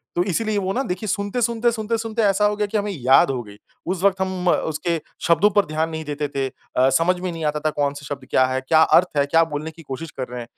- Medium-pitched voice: Yes, medium, 165 Hz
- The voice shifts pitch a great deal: Yes, wide, 5.8 semitones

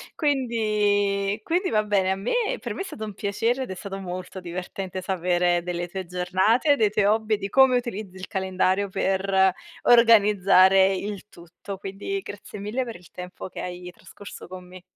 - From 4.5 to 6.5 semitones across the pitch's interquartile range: No, narrow, 2.6 semitones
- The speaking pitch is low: No, high, 195 Hz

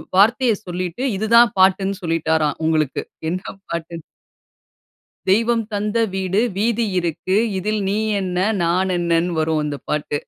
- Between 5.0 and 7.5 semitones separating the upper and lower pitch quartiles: No, average, 3.8 semitones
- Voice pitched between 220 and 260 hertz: No, medium, 185 Hz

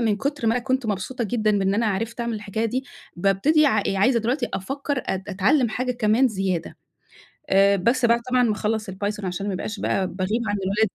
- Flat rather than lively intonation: No, average, 3.8 semitones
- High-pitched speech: Yes, high, 220 Hz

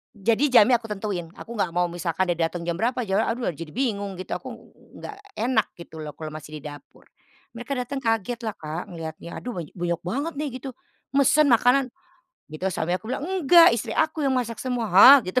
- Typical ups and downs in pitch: No, wide, 6.7 semitones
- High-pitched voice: Yes, high, 220 Hz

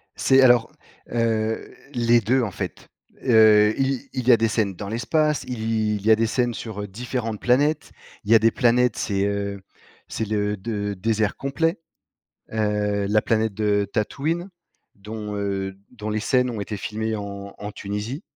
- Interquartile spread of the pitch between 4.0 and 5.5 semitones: No, average, 2.7 semitones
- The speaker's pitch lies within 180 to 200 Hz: No, low, 110 Hz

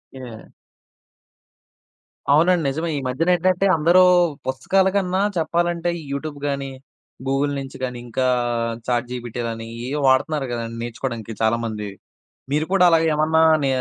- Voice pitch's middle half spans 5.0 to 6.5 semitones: Yes, average, 5.3 semitones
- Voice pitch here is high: No, medium, 140 Hz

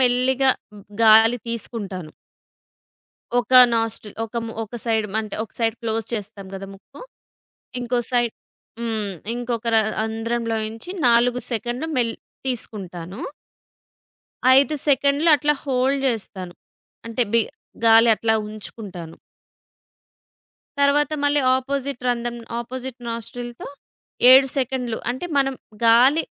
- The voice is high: Yes, high, 235 Hz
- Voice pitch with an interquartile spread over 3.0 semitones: No, average, 2.7 semitones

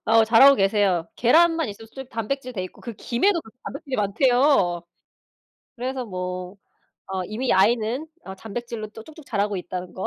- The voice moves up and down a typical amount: Yes, average, 5.0 semitones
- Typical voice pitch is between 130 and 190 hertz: No, high, 225 Hz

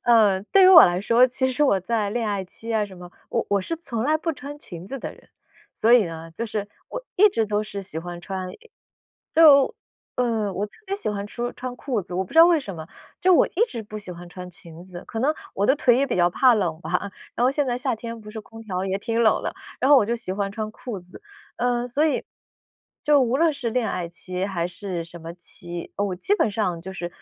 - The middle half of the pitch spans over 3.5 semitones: Yes, wide, 5.5 semitones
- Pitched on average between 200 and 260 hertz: Yes, high, 215 Hz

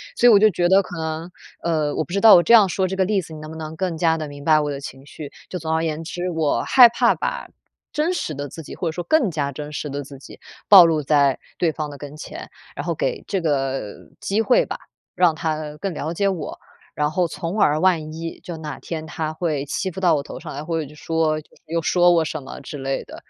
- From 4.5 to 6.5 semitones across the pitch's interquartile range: No, average, 3.3 semitones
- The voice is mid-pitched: Yes, medium, 160 Hz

